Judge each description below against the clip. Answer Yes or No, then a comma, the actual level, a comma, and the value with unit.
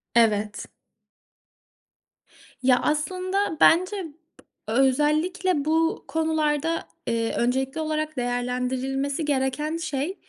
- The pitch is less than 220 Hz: No, very high, 295 Hz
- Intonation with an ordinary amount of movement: Yes, average, 4.1 semitones